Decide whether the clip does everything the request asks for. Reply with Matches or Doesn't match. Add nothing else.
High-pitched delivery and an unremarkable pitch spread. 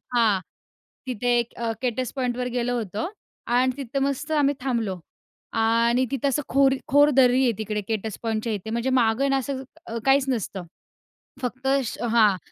Matches